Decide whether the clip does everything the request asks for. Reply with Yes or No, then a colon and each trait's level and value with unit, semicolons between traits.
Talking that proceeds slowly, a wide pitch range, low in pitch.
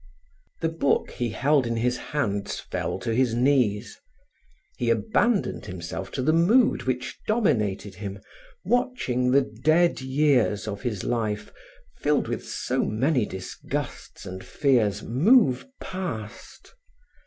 Yes: slow, 125 wpm; wide, 6.0 semitones; low, 125 Hz